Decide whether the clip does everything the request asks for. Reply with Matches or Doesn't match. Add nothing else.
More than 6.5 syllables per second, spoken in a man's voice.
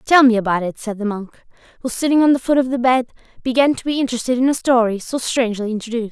Doesn't match